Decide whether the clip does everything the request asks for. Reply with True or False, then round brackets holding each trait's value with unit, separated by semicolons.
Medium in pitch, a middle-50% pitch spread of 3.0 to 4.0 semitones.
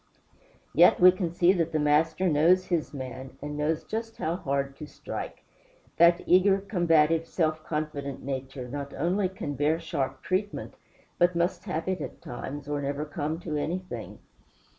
True (155 Hz; 3.5 semitones)